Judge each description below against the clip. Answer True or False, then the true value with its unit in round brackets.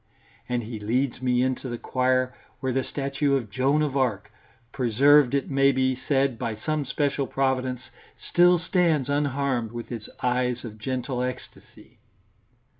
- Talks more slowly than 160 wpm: True (150 wpm)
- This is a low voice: True (130 Hz)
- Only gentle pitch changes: True (2.2 semitones)